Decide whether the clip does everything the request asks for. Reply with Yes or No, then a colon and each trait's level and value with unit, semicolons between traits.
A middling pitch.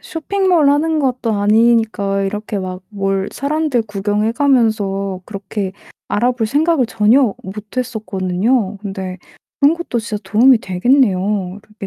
No: high, 215 Hz